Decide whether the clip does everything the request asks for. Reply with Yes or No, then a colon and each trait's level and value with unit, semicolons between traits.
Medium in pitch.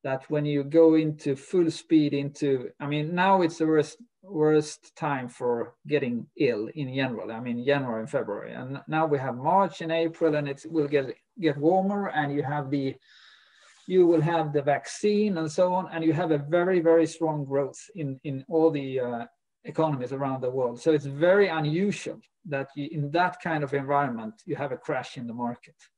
Yes: medium, 150 Hz